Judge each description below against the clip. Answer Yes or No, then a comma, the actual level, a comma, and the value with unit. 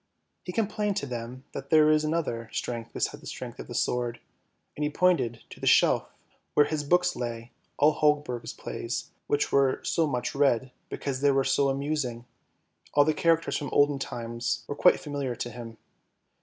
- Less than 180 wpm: No, average, 185 wpm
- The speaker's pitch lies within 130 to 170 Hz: Yes, medium, 140 Hz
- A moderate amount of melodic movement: Yes, average, 3.9 semitones